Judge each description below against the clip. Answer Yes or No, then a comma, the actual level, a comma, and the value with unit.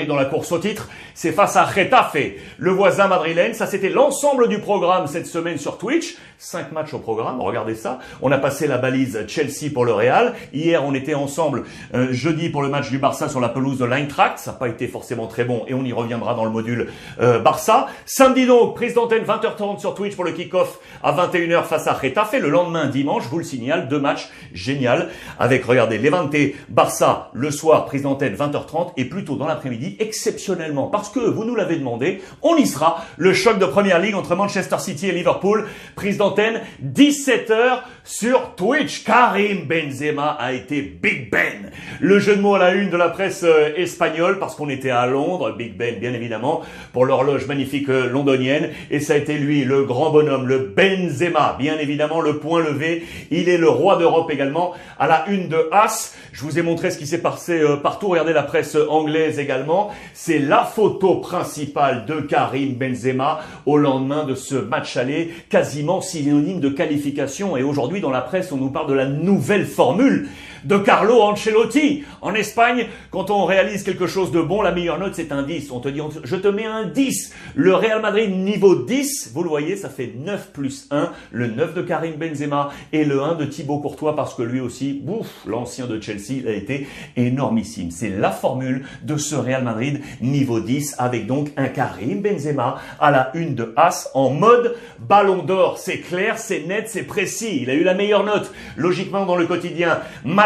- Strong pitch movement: Yes, wide, 6.0 semitones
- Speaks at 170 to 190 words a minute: No, average, 200 wpm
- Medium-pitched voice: Yes, medium, 160 Hz